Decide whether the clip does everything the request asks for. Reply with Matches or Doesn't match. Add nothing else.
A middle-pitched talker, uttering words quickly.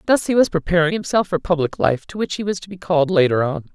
Matches